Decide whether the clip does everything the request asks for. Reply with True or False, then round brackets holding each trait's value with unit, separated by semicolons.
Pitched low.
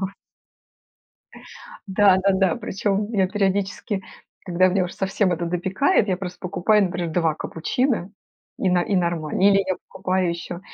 False (190 Hz)